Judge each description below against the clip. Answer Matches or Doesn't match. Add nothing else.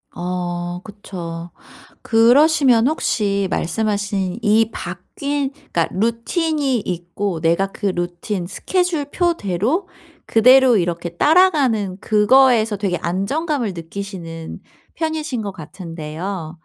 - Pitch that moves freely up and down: Matches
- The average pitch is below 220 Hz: Matches